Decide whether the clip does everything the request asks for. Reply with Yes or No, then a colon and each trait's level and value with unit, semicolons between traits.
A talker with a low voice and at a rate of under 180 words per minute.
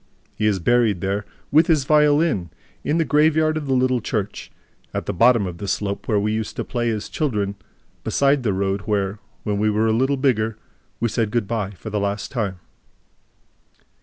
No: low, 110 Hz; average, 195 wpm